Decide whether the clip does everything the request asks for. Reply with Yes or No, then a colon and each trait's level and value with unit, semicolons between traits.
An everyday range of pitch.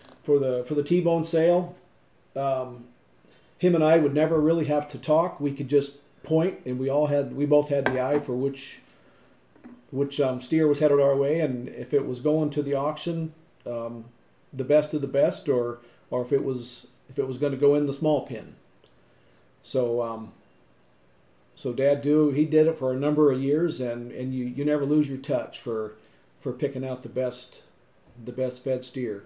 Yes: average, 3.1 semitones